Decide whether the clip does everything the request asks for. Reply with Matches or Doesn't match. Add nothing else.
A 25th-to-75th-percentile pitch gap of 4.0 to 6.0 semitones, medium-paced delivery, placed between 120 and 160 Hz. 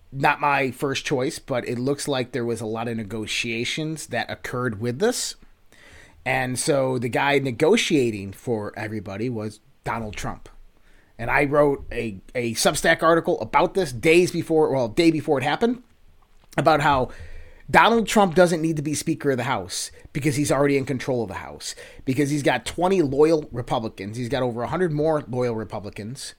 Matches